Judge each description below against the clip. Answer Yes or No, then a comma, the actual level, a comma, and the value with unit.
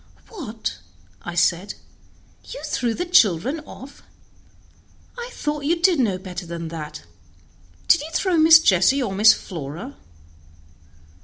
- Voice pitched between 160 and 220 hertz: No, high, 230 Hz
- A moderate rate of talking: No, slow, 130 wpm